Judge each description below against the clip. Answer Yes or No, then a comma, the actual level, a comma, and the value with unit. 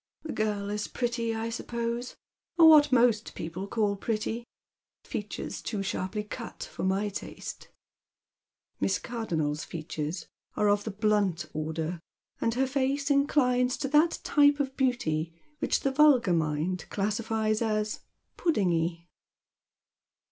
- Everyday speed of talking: No, slow, 130 wpm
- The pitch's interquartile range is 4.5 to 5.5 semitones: Yes, average, 5.1 semitones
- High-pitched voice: Yes, high, 215 Hz